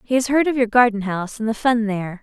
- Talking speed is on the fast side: Yes, fast, 295 wpm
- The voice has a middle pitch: No, high, 230 Hz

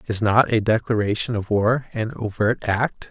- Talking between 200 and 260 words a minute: No, average, 175 wpm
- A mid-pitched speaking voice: No, low, 110 Hz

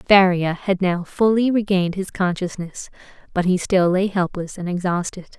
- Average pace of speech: Yes, average, 155 wpm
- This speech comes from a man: No, female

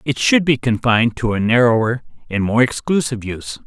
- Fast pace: No, average, 180 wpm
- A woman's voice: No, male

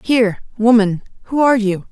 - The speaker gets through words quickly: No, average, 155 wpm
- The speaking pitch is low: No, high, 225 Hz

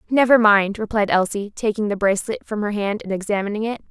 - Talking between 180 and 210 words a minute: Yes, average, 200 wpm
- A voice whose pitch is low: No, high, 210 Hz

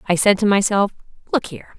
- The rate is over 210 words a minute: No, average, 200 wpm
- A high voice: Yes, high, 200 Hz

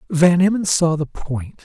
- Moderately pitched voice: Yes, medium, 165 Hz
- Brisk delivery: No, average, 185 wpm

